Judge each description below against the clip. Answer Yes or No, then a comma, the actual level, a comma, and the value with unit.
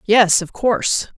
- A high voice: Yes, high, 205 Hz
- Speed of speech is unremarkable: Yes, average, 150 wpm